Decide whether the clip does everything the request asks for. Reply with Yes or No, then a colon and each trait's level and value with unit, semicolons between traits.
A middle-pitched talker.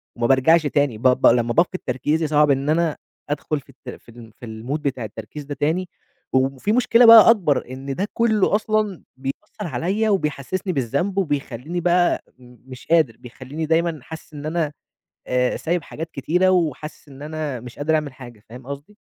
Yes: medium, 150 Hz